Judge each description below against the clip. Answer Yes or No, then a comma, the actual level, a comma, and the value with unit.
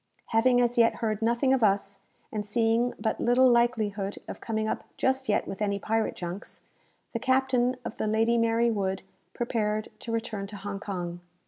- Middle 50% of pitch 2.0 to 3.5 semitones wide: Yes, average, 2.7 semitones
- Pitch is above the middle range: Yes, high, 225 Hz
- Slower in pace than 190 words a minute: Yes, average, 180 wpm